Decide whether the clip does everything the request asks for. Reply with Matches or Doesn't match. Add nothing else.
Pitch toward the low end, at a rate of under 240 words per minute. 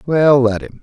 Matches